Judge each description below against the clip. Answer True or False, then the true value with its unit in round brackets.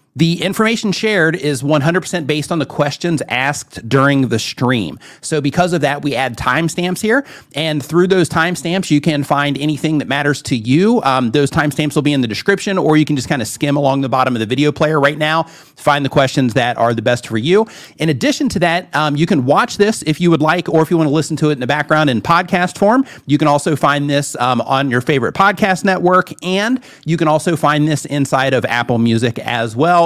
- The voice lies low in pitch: False (150 Hz)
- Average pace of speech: False (230 wpm)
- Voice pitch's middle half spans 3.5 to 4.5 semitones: True (3.8 semitones)